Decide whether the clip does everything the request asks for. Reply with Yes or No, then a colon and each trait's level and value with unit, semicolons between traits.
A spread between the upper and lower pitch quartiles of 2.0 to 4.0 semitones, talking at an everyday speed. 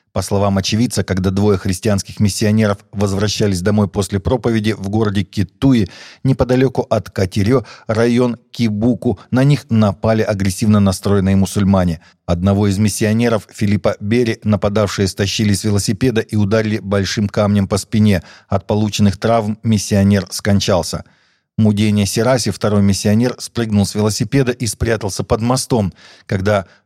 Yes: narrow, 2.4 semitones; average, 125 wpm